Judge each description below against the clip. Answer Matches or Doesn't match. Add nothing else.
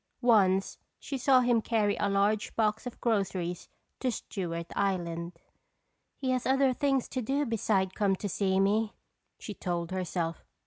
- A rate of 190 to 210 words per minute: Doesn't match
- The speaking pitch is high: Matches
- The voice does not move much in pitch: Doesn't match